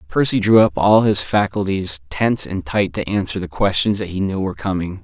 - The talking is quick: Yes, fast, 215 wpm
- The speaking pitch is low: Yes, very low, 95 Hz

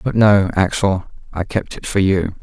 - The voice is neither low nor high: No, very low, 95 Hz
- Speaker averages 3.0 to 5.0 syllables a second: Yes, 4.6 syllables/s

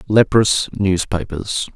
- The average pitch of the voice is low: Yes, very low, 95 Hz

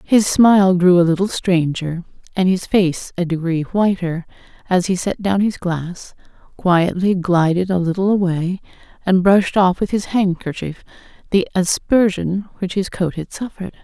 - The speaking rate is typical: Yes, average, 155 wpm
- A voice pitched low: No, medium, 185 Hz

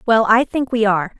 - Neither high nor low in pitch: No, high, 220 Hz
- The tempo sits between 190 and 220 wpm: No, fast, 250 wpm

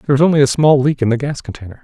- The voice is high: No, low, 135 Hz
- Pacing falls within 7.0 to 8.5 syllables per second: Yes, 7.8 syllables/s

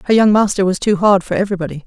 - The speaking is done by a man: No, female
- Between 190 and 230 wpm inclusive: No, fast, 290 wpm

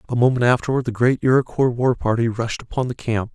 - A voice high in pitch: No, low, 120 Hz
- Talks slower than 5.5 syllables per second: No, 6.0 syllables/s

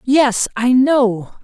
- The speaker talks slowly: Yes, slow, 125 wpm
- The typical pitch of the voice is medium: No, high, 245 Hz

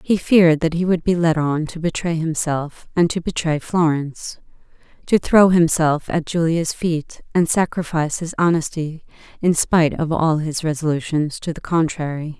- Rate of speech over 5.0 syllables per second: No, 4.8 syllables/s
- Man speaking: No, female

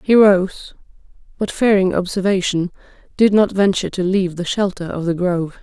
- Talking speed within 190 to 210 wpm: No, average, 160 wpm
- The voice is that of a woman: Yes, female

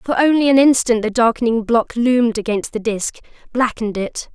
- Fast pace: No, average, 180 wpm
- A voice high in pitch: Yes, high, 235 Hz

